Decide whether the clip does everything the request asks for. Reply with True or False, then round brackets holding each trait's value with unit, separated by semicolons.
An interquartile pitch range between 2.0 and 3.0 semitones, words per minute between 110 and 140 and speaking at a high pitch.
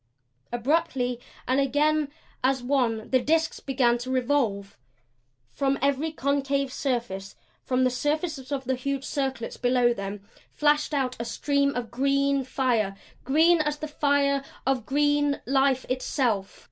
True (2.6 semitones; 135 wpm; 270 Hz)